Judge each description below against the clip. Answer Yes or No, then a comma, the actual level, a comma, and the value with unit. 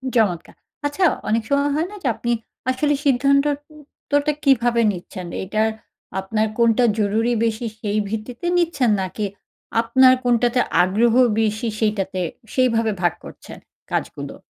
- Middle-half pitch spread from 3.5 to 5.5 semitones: Yes, average, 3.9 semitones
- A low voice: No, high, 235 Hz